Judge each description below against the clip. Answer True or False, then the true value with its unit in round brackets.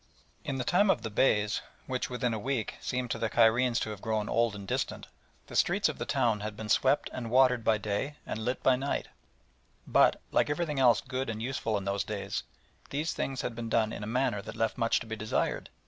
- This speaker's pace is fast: True (225 wpm)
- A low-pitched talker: True (115 Hz)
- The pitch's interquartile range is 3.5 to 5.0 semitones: False (3.0 semitones)